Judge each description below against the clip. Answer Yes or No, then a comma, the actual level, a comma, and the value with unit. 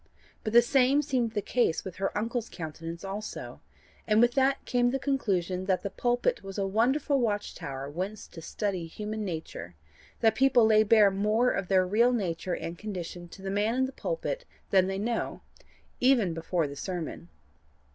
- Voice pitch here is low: No, high, 210 Hz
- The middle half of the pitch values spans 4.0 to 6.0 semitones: Yes, average, 4.8 semitones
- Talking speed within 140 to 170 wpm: No, average, 180 wpm